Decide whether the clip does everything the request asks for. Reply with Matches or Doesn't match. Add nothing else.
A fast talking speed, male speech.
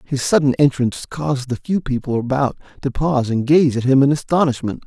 Doesn't match